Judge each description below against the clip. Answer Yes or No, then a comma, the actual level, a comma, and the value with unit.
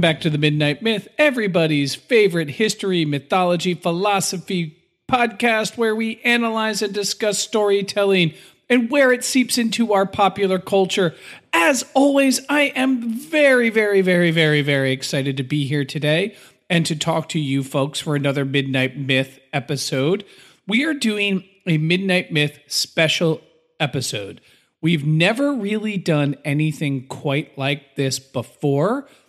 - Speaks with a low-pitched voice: No, medium, 180 Hz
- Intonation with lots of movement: Yes, wide, 6.7 semitones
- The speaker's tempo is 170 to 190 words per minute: No, slow, 135 wpm